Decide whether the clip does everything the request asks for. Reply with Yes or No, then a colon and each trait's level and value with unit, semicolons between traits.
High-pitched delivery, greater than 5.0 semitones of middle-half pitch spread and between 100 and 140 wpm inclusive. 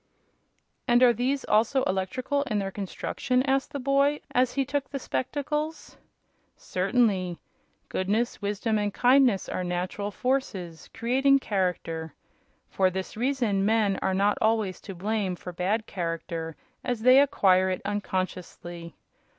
Yes: high, 210 Hz; wide, 5.6 semitones; slow, 135 wpm